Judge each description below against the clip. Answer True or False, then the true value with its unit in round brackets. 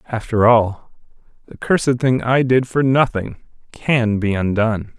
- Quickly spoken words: False (145 wpm)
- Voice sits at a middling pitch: False (120 Hz)